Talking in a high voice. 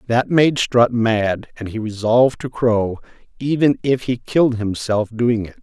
No: low, 115 Hz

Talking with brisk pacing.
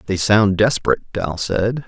No: average, 160 wpm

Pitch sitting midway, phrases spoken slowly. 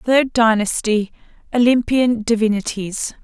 No: high, 230 Hz; slow, 55 wpm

